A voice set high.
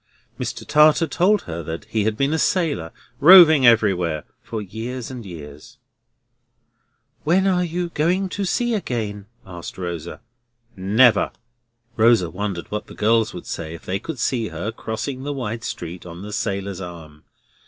No: low, 110 Hz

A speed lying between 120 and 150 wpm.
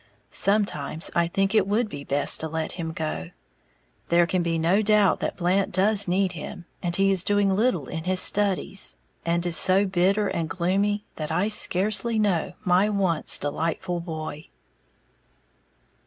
No: average, 160 wpm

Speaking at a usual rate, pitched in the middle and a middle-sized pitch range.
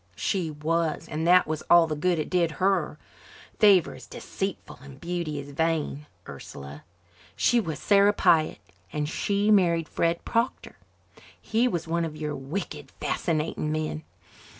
Yes: average, 150 wpm; medium, 165 Hz; average, 3.1 semitones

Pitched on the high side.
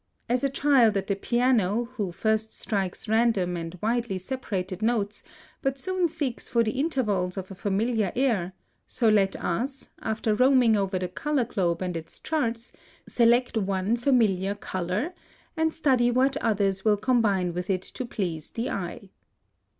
Yes: high, 220 Hz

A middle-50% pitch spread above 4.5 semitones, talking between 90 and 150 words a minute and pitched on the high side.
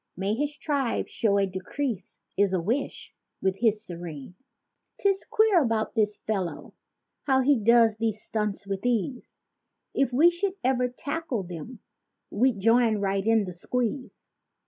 Yes: average, 5.0 semitones; average, 145 wpm; high, 225 Hz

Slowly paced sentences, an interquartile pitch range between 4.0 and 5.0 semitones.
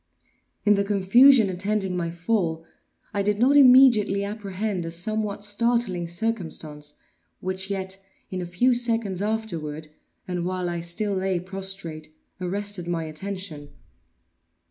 No: slow, 125 wpm; average, 3.4 semitones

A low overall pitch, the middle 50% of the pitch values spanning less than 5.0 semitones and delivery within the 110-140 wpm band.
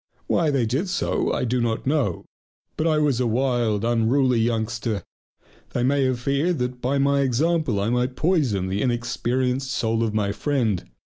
No: low, 125 Hz; average, 3.4 semitones; average, 170 wpm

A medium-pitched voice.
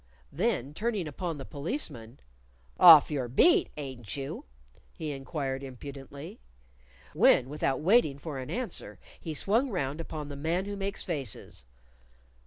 Yes: medium, 150 Hz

